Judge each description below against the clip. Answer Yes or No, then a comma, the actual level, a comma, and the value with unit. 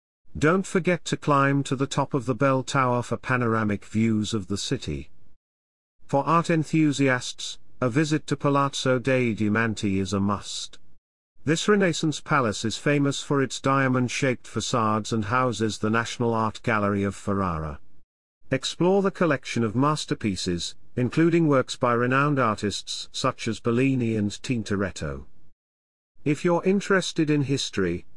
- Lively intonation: Yes, wide, 5.9 semitones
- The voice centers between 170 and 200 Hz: No, low, 125 Hz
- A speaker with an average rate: Yes, average, 145 wpm